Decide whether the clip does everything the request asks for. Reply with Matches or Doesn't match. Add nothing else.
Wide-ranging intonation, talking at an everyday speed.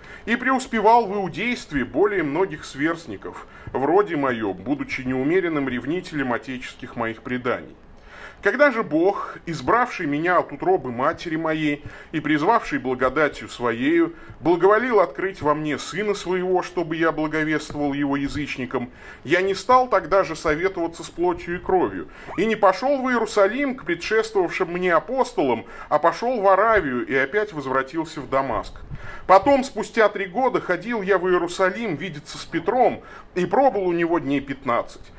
Matches